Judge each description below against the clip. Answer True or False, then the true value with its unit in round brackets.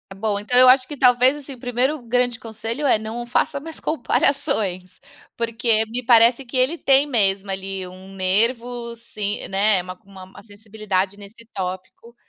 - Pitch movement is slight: False (4.1 semitones)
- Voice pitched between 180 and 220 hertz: False (230 Hz)